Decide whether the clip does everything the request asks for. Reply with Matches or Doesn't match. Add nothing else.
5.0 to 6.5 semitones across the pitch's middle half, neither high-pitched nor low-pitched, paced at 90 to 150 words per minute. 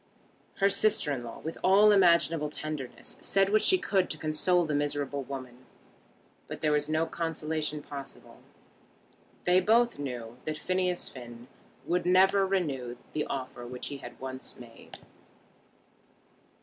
Matches